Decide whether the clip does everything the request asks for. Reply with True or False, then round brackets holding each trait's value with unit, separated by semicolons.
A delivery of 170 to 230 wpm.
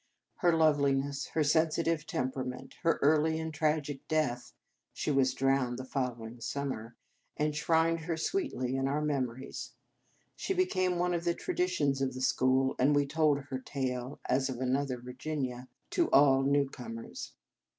False (155 wpm)